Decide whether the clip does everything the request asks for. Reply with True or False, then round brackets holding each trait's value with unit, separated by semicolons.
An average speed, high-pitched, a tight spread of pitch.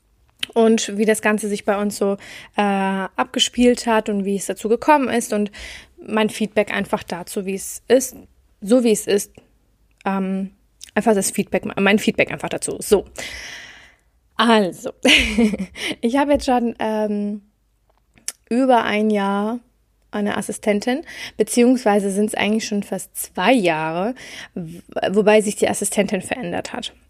True (140 wpm; 215 Hz; 2.3 semitones)